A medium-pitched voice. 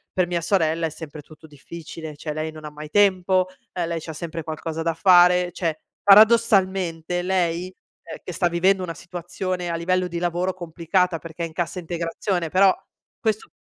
Yes: medium, 175 Hz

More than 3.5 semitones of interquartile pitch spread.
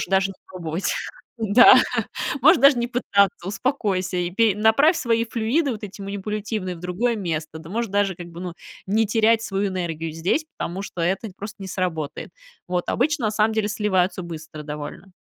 Yes: average, 3.9 semitones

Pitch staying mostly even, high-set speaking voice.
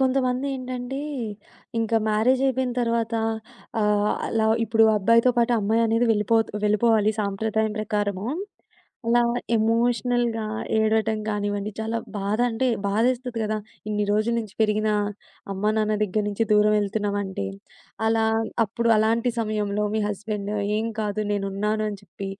Yes: narrow, 1.8 semitones; high, 220 Hz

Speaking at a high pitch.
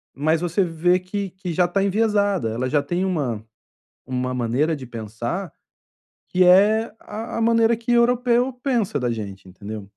No: medium, 180 Hz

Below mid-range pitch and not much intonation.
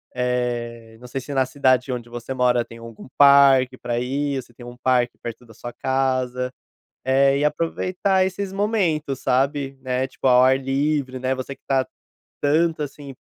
Yes: low, 130 Hz; narrow, 2.2 semitones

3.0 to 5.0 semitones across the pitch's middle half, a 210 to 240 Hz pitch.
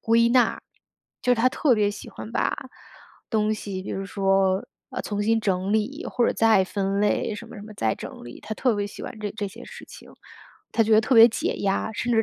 No: narrow, 2.4 semitones; high, 215 Hz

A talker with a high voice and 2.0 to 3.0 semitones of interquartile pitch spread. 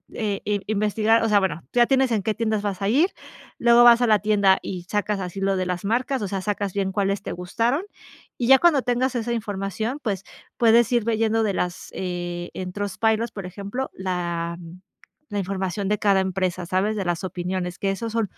No: high, 205 Hz; average, 3.4 semitones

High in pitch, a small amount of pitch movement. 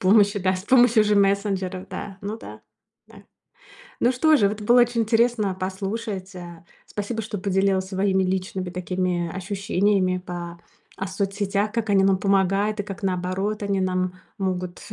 Yes: high, 195 Hz; narrow, 2.1 semitones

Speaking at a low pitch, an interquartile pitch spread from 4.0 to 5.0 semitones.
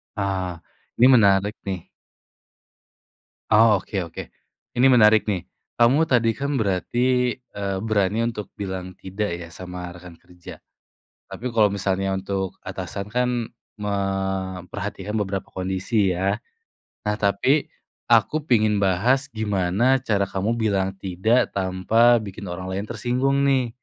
No: low, 100 Hz; average, 3.6 semitones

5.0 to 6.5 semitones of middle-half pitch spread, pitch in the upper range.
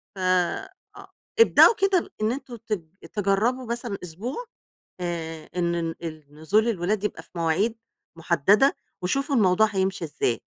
Yes: wide, 5.5 semitones; high, 195 Hz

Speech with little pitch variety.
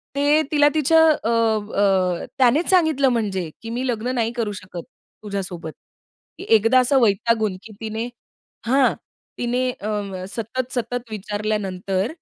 No: average, 4.0 semitones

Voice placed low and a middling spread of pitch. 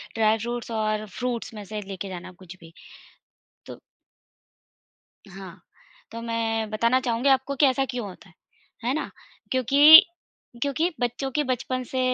No: high, 230 Hz; average, 3.5 semitones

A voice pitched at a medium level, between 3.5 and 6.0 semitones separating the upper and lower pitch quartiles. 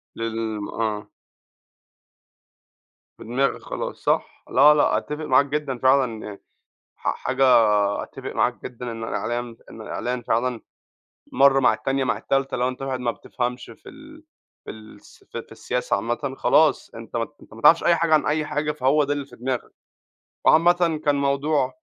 No: low, 130 Hz; average, 3.8 semitones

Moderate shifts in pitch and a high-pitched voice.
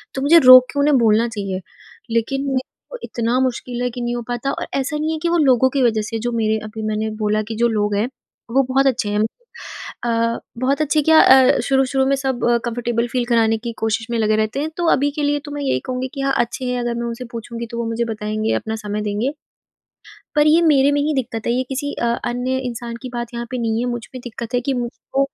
Yes: average, 3.0 semitones; high, 240 Hz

